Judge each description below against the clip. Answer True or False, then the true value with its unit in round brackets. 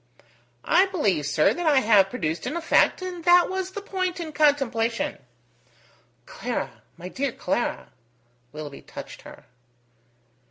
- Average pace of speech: False (130 wpm)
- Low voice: False (290 Hz)